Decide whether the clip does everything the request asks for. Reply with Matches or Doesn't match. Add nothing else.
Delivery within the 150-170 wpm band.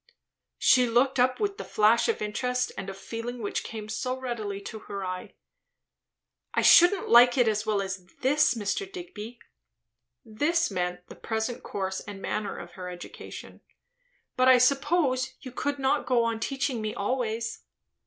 Matches